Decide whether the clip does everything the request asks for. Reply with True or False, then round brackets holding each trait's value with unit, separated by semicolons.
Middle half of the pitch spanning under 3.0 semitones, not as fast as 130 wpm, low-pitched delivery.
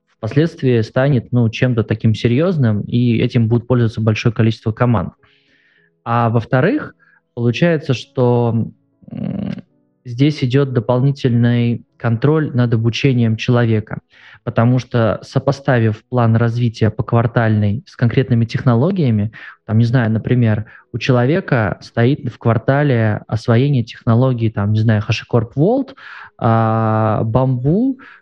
True (2.6 semitones; 110 wpm; 120 Hz)